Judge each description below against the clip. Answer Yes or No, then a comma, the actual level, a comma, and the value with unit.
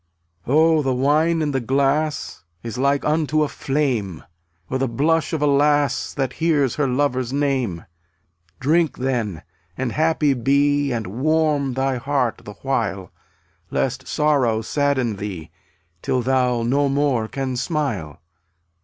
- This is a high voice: No, low, 135 Hz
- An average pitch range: Yes, average, 3.2 semitones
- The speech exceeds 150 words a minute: No, average, 145 wpm